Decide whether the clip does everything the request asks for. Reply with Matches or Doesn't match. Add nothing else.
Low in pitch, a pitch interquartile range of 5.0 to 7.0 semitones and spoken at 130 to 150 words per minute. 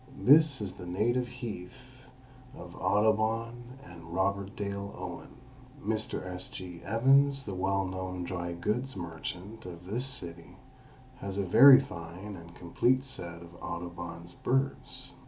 Matches